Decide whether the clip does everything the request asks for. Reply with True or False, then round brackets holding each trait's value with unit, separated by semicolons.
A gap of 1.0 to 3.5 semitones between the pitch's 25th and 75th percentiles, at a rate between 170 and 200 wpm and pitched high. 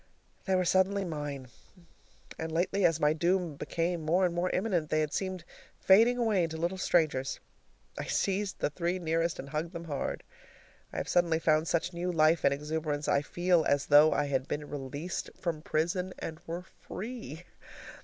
False (3.0 semitones; 175 wpm; 165 Hz)